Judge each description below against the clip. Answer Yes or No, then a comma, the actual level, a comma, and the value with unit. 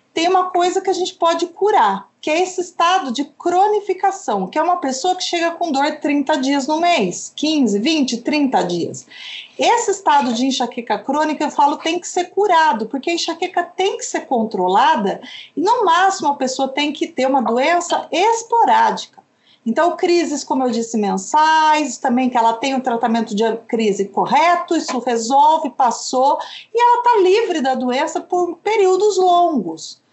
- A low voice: No, very high, 310 Hz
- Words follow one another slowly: No, average, 175 wpm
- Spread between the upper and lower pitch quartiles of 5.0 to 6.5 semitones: Yes, wide, 5.5 semitones